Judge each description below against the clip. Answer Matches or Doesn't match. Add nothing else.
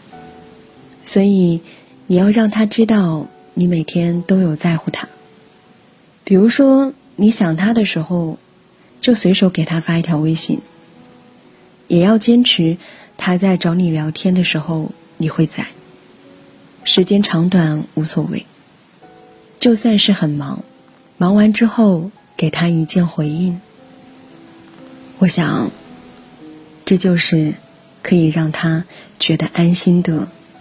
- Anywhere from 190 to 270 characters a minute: Doesn't match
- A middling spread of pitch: Matches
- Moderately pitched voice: Matches